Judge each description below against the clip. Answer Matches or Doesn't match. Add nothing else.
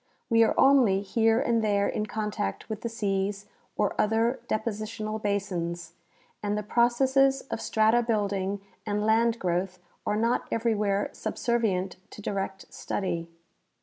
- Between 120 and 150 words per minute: Matches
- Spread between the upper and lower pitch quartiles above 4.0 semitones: Doesn't match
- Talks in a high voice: Matches